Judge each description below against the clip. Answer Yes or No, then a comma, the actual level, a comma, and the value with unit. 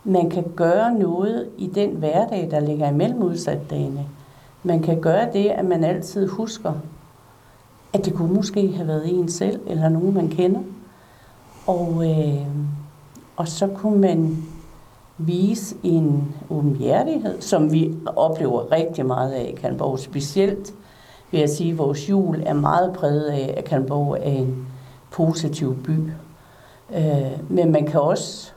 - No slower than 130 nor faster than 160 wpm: Yes, slow, 145 wpm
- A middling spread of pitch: Yes, average, 4.5 semitones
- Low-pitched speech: No, medium, 160 Hz